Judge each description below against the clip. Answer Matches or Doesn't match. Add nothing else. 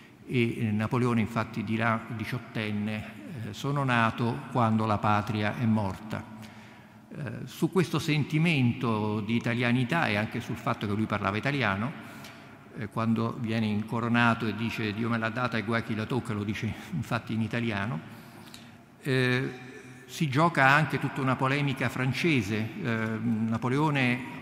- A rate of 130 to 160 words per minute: Matches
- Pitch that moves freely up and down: Doesn't match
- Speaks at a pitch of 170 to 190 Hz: Doesn't match